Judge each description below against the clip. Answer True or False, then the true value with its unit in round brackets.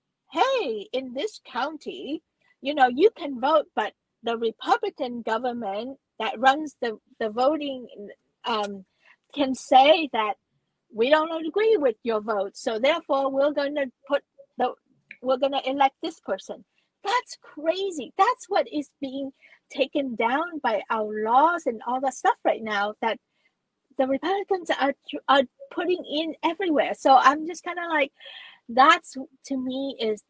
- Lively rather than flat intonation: False (3.9 semitones)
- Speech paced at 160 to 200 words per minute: False (150 wpm)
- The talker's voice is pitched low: False (270 Hz)